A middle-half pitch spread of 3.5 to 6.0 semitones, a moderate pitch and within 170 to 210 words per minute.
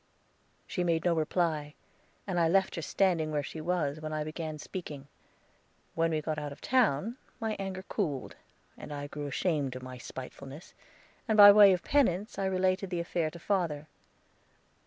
Yes: average, 4.0 semitones; medium, 165 Hz; average, 175 wpm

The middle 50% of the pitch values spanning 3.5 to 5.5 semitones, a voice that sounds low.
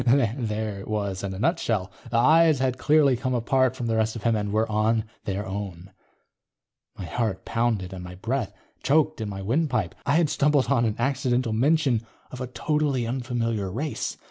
Yes: average, 4.3 semitones; low, 115 Hz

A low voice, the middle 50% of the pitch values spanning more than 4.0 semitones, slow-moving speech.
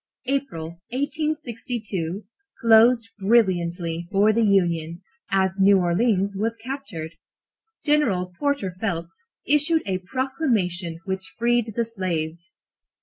No: high, 200 Hz; average, 5.3 semitones; slow, 100 wpm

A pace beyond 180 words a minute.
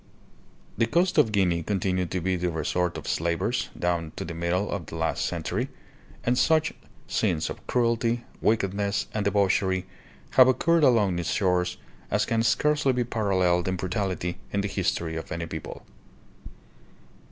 No: average, 155 wpm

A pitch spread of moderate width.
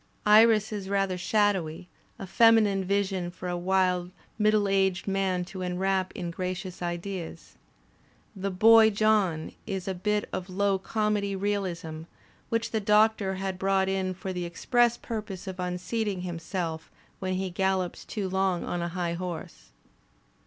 No: narrow, 2.2 semitones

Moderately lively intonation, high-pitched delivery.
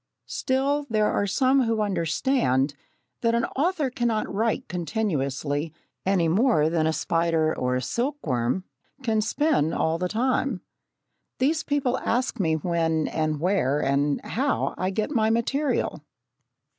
No: wide, 8.0 semitones; high, 200 Hz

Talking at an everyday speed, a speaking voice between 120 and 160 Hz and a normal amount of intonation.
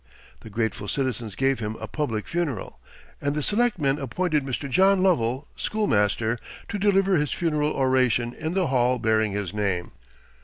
No: average, 155 wpm; low, 135 Hz; wide, 6.7 semitones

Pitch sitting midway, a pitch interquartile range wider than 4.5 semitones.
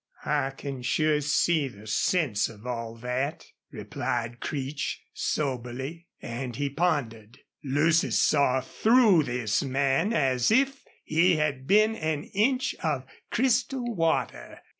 Yes: medium, 145 Hz; wide, 5.4 semitones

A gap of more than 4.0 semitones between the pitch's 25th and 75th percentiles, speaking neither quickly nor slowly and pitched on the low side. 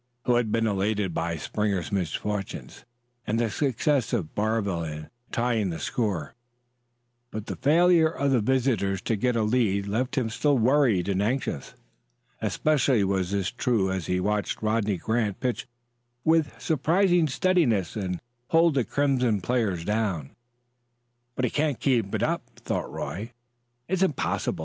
Yes: average, 5.1 semitones; average, 150 wpm; low, 110 Hz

